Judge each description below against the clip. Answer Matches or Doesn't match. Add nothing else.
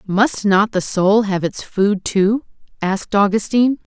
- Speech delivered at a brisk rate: Doesn't match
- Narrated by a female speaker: Matches